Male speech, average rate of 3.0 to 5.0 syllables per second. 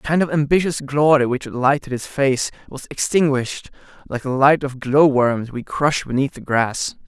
Yes: male; 4.9 syllables/s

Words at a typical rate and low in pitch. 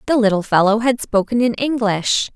No: average, 180 wpm; high, 220 Hz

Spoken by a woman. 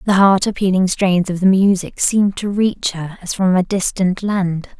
Yes: female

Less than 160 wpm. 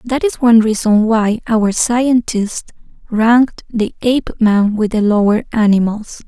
Yes: slow, 135 wpm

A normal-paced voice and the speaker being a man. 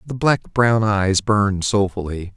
Yes: average, 155 wpm; male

